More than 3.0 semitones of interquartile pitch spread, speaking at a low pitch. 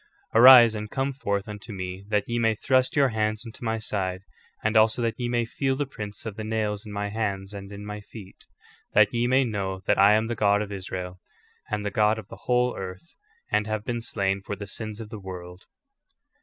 No: narrow, 2.4 semitones; low, 105 Hz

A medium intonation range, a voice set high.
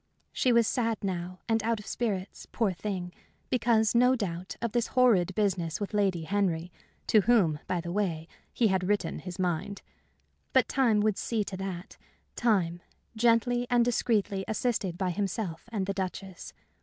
Yes: average, 3.9 semitones; high, 200 Hz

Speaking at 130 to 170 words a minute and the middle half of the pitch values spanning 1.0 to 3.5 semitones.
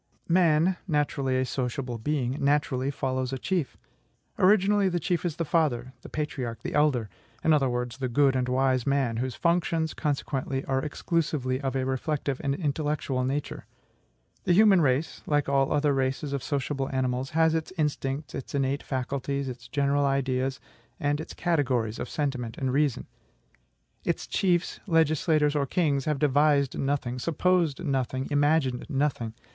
Yes: average, 155 wpm; average, 2.8 semitones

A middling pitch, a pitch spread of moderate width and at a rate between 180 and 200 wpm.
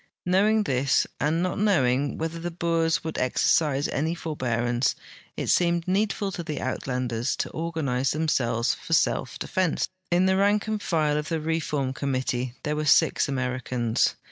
No: medium, 155 Hz; average, 4.9 semitones; average, 160 wpm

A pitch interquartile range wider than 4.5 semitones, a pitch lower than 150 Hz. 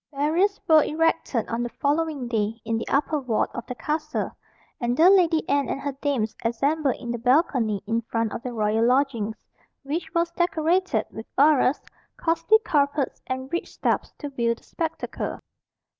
No: average, 5.2 semitones; very high, 275 Hz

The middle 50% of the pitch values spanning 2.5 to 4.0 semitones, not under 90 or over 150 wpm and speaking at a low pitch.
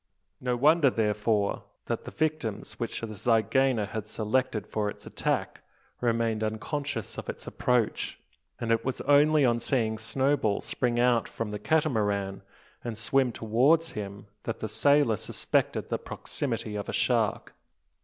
Yes: average, 3.6 semitones; average, 145 wpm; low, 115 Hz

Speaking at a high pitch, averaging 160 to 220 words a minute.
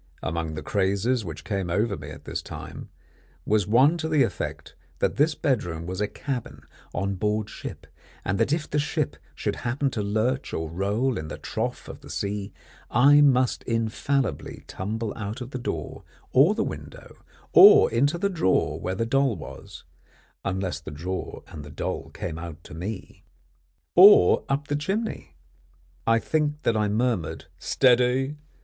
No: low, 110 Hz; average, 170 wpm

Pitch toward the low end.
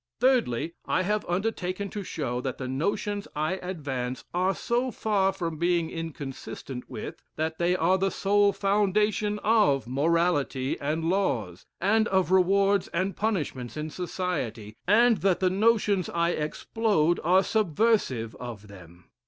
No: medium, 180 Hz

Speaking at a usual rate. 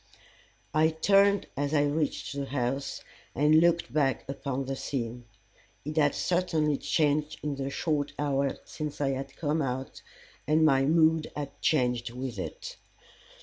Yes: average, 145 wpm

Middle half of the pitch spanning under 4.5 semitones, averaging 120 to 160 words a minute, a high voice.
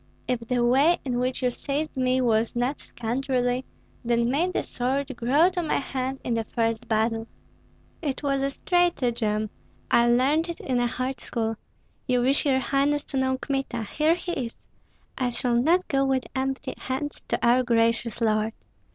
No: narrow, 2.6 semitones; average, 175 wpm; very high, 255 Hz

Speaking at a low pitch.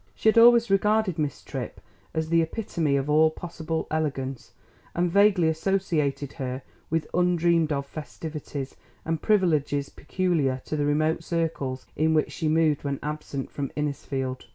No: medium, 155 Hz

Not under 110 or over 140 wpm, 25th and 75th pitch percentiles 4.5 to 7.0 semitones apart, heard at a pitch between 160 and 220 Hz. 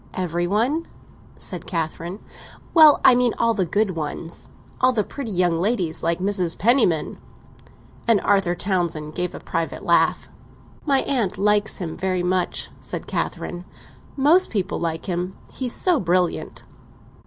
Yes: slow, 135 wpm; average, 5.0 semitones; medium, 185 Hz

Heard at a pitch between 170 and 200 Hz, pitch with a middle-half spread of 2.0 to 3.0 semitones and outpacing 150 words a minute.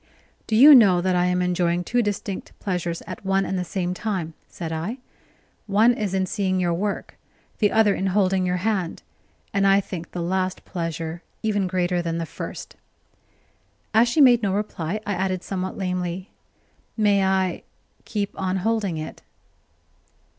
Yes: high, 190 Hz; narrow, 2.4 semitones; average, 165 wpm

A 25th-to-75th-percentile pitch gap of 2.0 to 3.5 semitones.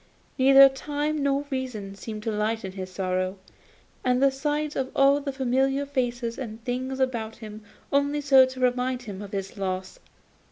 No: average, 4.2 semitones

